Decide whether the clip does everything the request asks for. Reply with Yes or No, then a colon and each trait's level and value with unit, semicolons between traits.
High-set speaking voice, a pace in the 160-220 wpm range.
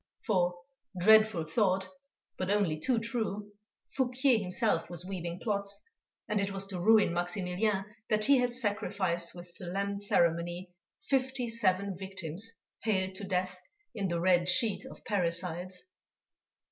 No: high, 195 Hz; slow, 135 wpm